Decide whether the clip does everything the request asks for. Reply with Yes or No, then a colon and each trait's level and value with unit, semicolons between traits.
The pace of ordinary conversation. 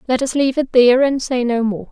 No: fast, 280 wpm